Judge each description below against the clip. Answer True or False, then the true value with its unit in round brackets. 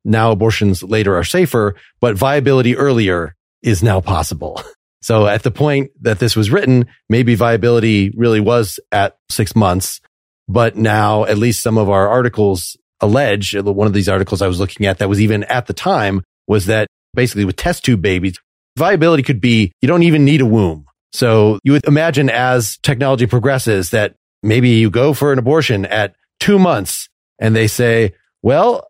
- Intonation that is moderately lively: True (3.8 semitones)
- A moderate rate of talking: True (180 wpm)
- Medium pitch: False (110 Hz)